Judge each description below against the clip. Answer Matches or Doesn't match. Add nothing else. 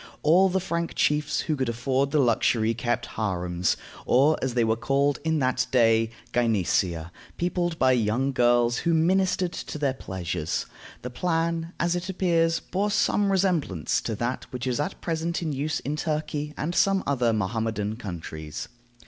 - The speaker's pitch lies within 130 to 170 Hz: Matches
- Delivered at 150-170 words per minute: Matches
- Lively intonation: Matches